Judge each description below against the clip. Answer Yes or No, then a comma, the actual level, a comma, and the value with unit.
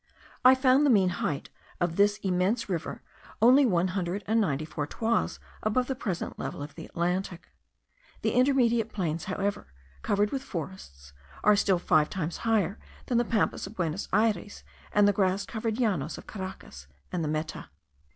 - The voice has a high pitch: Yes, high, 195 Hz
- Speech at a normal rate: Yes, average, 170 wpm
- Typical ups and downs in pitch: Yes, average, 4.6 semitones